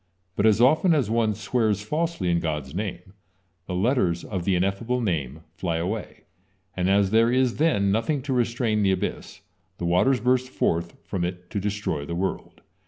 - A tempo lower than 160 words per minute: No, average, 175 wpm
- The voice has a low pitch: Yes, low, 100 Hz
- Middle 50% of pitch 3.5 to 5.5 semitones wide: Yes, average, 5.2 semitones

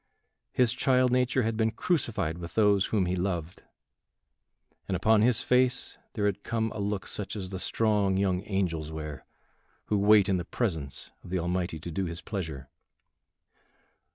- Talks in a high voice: No, low, 100 Hz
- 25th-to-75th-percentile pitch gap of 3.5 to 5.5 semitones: Yes, average, 4.1 semitones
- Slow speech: No, average, 165 wpm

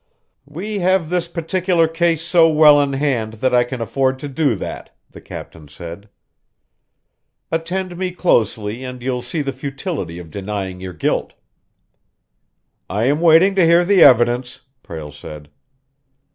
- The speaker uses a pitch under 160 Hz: Yes, low, 135 Hz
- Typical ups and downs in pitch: No, wide, 7.4 semitones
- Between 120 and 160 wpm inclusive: Yes, average, 145 wpm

